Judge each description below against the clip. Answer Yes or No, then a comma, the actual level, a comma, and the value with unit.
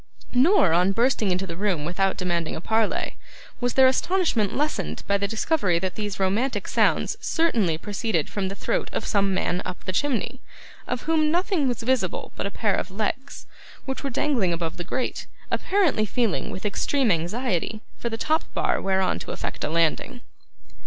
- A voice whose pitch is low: No, high, 210 Hz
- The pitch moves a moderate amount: No, wide, 6.0 semitones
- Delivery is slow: No, average, 180 wpm